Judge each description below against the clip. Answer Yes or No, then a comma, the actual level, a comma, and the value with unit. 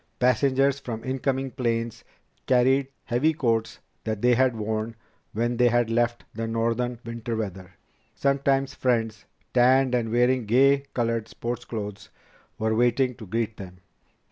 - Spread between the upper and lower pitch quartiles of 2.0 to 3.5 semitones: Yes, narrow, 2.4 semitones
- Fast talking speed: No, average, 140 wpm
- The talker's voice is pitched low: Yes, low, 120 Hz